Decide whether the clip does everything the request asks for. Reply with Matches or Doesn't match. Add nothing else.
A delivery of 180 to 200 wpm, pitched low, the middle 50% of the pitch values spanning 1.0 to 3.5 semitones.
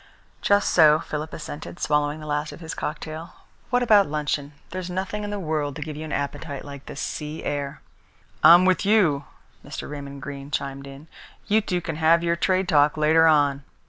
Doesn't match